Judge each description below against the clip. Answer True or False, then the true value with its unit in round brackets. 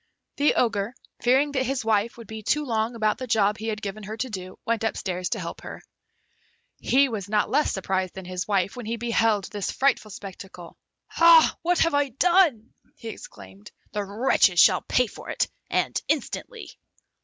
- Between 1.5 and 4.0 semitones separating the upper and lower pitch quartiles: False (4.4 semitones)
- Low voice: False (220 Hz)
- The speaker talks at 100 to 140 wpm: False (185 wpm)